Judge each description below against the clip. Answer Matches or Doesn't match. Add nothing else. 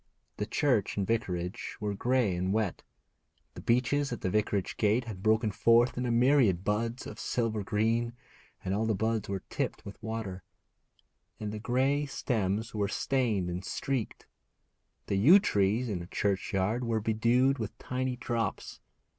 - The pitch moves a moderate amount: Matches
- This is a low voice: Matches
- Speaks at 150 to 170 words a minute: Matches